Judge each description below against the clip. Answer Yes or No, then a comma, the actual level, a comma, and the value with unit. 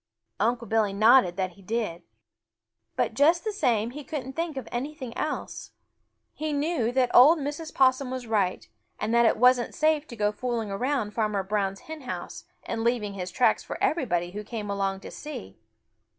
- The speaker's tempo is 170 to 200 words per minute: Yes, average, 180 wpm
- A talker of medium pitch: No, high, 235 Hz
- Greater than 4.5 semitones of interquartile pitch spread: Yes, average, 5.0 semitones